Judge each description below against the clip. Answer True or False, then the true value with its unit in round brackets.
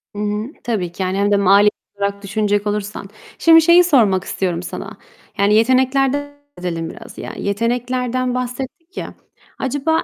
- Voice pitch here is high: True (215 Hz)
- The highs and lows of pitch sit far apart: False (4.6 semitones)